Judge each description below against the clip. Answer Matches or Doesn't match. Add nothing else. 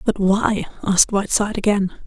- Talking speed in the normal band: Matches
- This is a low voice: Doesn't match